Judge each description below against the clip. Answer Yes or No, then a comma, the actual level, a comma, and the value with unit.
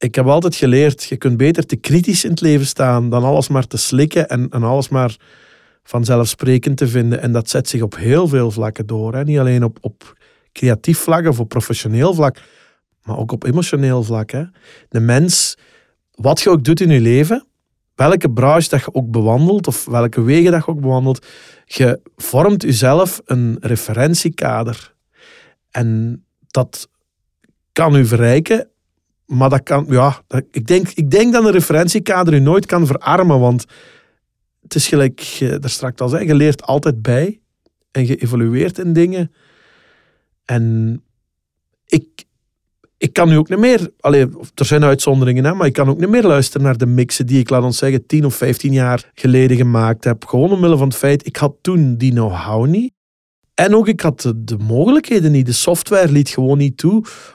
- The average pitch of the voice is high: No, low, 135 Hz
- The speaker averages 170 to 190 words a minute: Yes, average, 180 wpm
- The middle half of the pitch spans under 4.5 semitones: No, average, 4.8 semitones